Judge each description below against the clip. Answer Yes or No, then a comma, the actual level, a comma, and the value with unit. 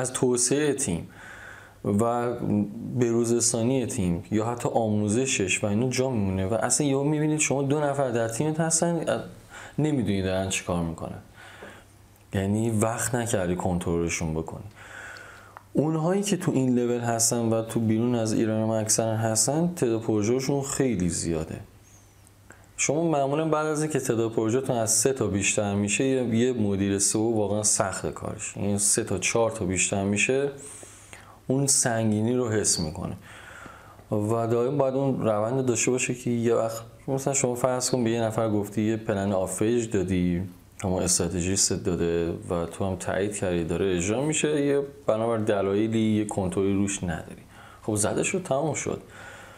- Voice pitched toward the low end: Yes, low, 110 Hz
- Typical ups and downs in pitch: Yes, average, 4.2 semitones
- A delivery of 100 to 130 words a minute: No, average, 150 wpm